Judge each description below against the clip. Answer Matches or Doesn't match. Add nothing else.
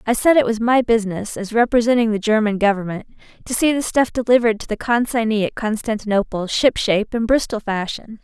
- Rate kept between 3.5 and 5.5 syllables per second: Doesn't match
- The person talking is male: Doesn't match